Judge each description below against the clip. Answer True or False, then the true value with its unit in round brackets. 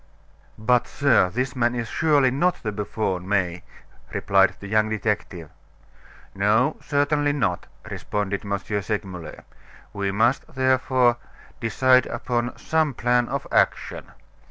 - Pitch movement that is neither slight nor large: True (4.5 semitones)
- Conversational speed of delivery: False (120 wpm)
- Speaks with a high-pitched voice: False (115 Hz)